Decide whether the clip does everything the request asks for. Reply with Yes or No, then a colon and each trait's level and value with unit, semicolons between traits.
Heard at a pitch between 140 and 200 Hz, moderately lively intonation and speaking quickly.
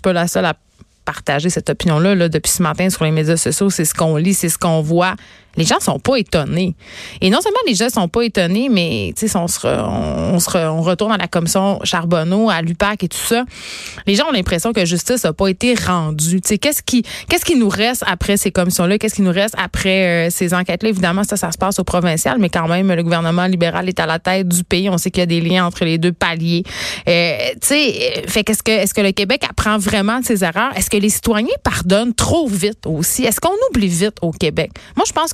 Yes: medium, 185 Hz; average, 3.8 semitones; fast, 245 wpm